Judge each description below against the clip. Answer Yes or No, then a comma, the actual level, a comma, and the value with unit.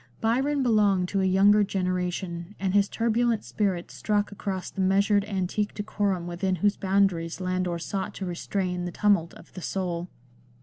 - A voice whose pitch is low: No, high, 195 Hz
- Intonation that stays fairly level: Yes, narrow, 2.3 semitones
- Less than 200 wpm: Yes, average, 160 wpm